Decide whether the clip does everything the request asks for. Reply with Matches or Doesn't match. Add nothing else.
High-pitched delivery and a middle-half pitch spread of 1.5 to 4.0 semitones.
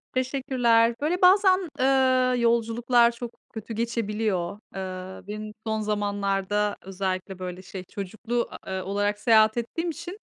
Matches